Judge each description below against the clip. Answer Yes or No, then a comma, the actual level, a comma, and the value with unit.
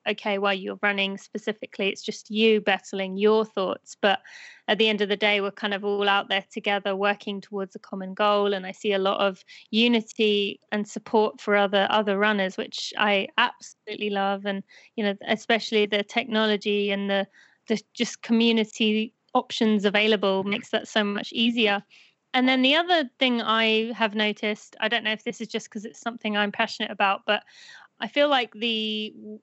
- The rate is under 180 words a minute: No, average, 190 wpm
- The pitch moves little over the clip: Yes, narrow, 1.8 semitones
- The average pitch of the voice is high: Yes, high, 215 Hz